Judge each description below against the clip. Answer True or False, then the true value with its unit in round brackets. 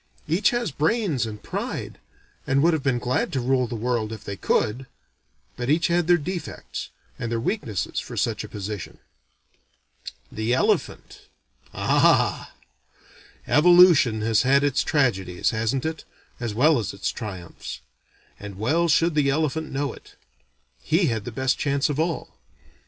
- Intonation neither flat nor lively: False (6.0 semitones)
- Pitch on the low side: True (130 Hz)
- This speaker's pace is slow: False (150 wpm)